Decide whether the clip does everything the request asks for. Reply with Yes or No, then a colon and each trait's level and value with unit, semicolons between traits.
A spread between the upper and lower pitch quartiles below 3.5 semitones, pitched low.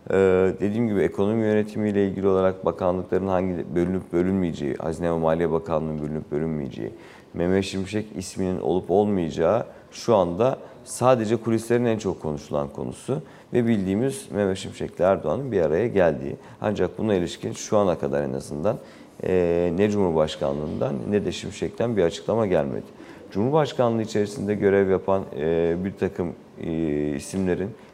No: average, 3.9 semitones; very low, 95 Hz